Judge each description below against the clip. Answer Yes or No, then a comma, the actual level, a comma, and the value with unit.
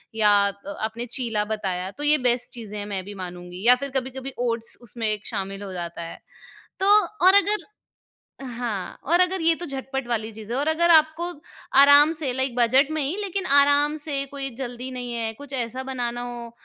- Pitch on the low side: No, very high, 250 Hz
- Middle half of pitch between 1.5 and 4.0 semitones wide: No, average, 4.6 semitones